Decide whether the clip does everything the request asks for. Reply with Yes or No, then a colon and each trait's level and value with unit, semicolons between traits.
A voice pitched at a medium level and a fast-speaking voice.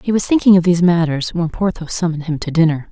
Yes: medium, 170 Hz; fast, 245 wpm